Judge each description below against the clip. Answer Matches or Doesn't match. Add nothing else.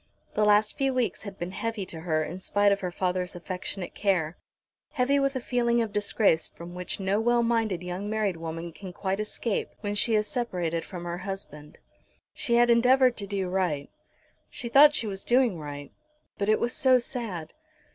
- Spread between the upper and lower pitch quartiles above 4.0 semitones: Matches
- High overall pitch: Matches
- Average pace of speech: Matches